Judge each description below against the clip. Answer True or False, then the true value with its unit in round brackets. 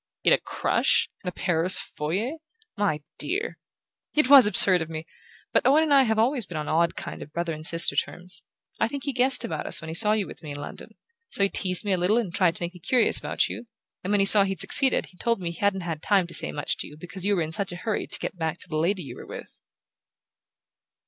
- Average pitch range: True (4.6 semitones)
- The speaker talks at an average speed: False (260 wpm)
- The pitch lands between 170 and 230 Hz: True (185 Hz)